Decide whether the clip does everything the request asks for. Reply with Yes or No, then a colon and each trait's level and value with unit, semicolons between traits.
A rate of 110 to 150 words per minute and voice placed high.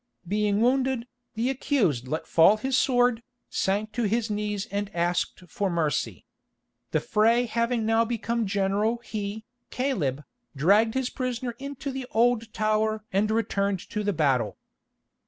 Yes: average, 140 wpm; high, 215 Hz